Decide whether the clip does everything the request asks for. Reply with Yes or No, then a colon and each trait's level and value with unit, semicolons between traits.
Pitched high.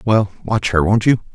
No: low, 105 Hz